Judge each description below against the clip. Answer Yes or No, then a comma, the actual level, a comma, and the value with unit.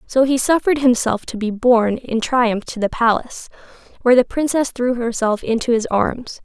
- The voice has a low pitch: No, high, 240 Hz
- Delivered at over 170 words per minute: Yes, average, 185 wpm